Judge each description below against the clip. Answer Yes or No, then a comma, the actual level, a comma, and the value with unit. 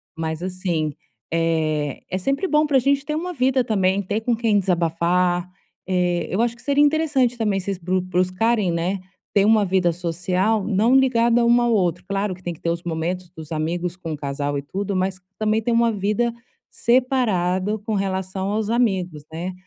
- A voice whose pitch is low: No, high, 190 Hz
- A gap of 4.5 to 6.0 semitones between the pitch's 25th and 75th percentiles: Yes, average, 4.8 semitones